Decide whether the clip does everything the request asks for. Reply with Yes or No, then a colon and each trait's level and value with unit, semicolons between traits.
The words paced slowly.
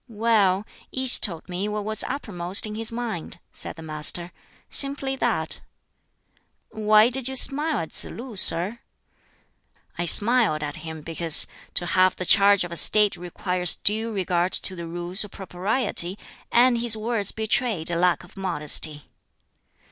No: average, 155 wpm